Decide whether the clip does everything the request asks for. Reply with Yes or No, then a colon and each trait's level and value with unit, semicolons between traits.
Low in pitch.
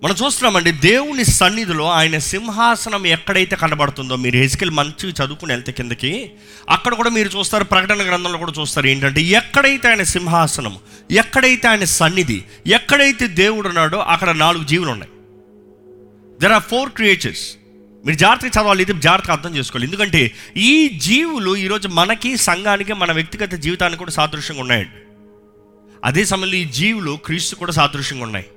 No: medium, 175 Hz